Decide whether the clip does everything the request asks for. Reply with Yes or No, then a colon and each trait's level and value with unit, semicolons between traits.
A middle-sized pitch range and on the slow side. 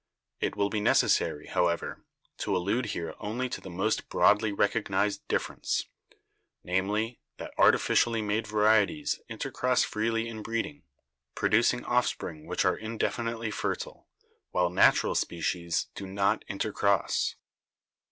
Yes: average, 3.0 semitones; slow, 125 wpm